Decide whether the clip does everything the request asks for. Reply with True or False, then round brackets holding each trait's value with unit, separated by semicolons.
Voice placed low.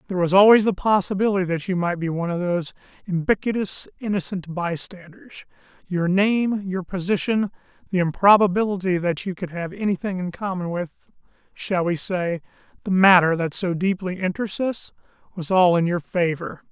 False (185 Hz)